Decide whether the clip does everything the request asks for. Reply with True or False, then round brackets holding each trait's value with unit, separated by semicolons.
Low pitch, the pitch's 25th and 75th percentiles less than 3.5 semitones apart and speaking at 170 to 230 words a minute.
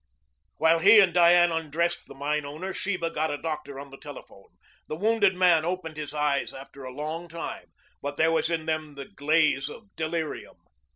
False (160 Hz; 2.8 semitones; 185 wpm)